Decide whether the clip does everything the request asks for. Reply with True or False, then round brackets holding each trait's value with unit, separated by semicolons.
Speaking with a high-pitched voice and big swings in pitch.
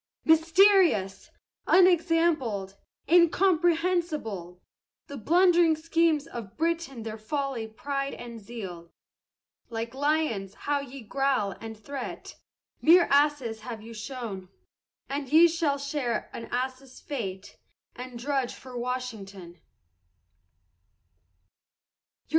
True (270 Hz; 6.3 semitones)